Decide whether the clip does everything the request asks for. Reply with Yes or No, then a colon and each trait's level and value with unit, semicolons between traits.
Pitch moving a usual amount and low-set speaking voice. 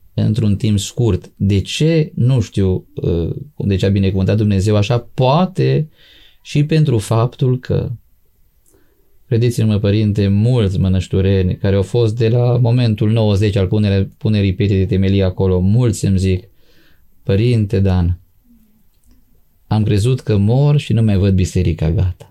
Yes: average, 3.9 semitones; low, 105 Hz